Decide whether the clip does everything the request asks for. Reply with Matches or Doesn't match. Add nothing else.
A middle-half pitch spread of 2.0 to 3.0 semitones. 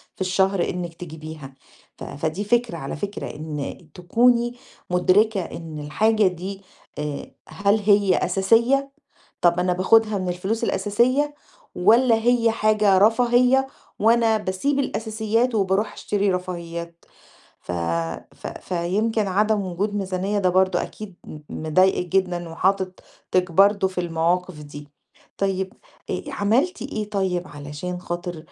Doesn't match